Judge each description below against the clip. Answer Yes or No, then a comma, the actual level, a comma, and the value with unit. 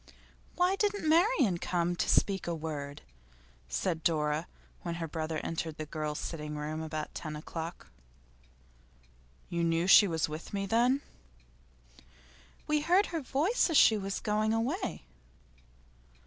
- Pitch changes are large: Yes, wide, 8.2 semitones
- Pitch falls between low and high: Yes, medium, 170 Hz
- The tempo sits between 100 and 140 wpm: Yes, slow, 135 wpm